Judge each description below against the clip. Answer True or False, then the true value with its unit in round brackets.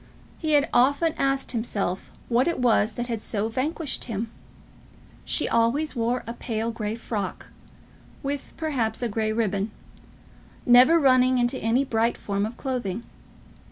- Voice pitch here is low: False (240 Hz)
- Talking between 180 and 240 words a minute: False (145 wpm)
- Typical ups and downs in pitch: True (3.2 semitones)